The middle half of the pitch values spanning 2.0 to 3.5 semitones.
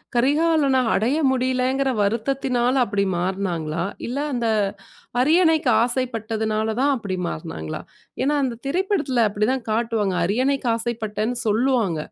No: average, 4.1 semitones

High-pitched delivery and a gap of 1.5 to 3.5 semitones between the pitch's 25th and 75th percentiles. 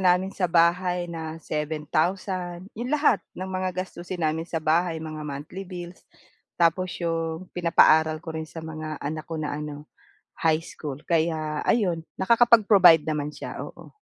No: medium, 165 Hz; narrow, 2.6 semitones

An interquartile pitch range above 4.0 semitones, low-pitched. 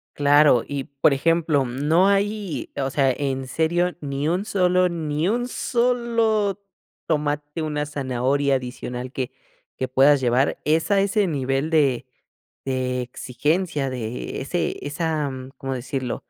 No: average, 4.7 semitones; medium, 145 Hz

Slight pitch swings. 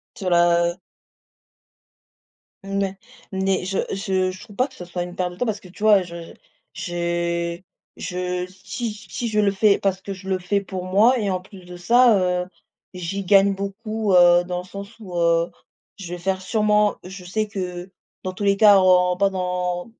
Yes: narrow, 2.0 semitones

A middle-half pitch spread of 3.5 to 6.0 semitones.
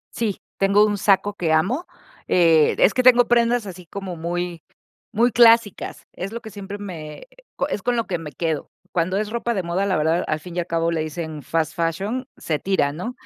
Yes: average, 4.6 semitones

